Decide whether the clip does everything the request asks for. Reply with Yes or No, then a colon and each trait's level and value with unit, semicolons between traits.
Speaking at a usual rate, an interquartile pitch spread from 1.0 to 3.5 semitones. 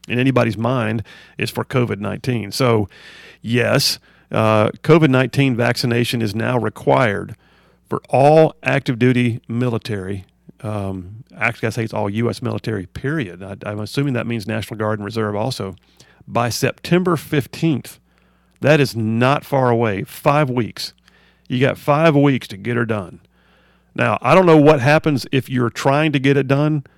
No: average, 160 wpm; average, 4.3 semitones